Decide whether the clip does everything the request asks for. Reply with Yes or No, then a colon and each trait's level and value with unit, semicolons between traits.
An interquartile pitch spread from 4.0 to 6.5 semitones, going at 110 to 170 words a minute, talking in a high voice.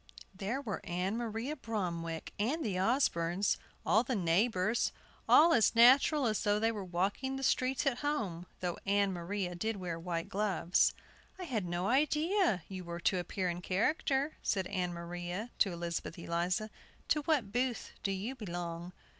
Yes: wide, 5.5 semitones; average, 165 wpm; high, 200 Hz